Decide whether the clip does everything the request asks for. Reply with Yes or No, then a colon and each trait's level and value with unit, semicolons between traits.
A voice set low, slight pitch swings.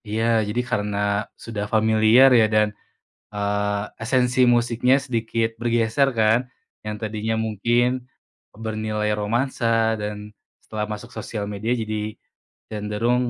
Yes: low, 110 Hz; narrow, 1.9 semitones